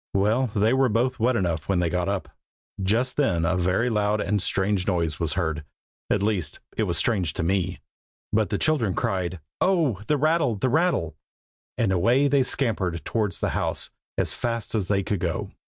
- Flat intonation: No, average, 4.9 semitones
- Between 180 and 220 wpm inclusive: Yes, average, 190 wpm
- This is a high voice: No, low, 100 Hz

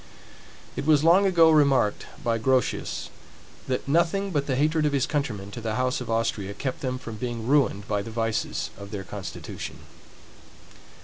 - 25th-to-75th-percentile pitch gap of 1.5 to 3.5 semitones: No, average, 4.9 semitones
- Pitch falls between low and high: No, low, 130 Hz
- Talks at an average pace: Yes, average, 170 wpm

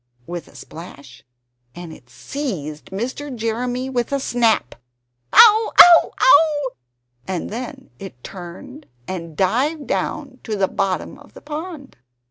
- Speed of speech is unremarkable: No, slow, 130 wpm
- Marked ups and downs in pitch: Yes, wide, 7.7 semitones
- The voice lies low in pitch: No, high, 245 Hz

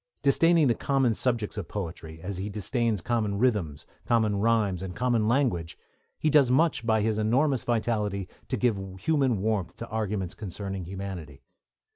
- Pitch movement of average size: Yes, average, 3.9 semitones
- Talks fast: No, average, 155 wpm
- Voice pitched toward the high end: No, low, 110 Hz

